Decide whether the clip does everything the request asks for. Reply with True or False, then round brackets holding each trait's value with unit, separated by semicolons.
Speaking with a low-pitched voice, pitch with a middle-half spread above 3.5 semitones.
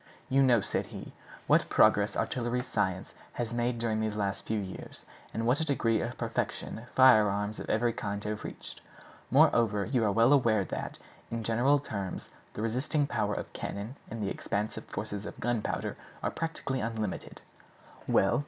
False (115 Hz; 2.7 semitones)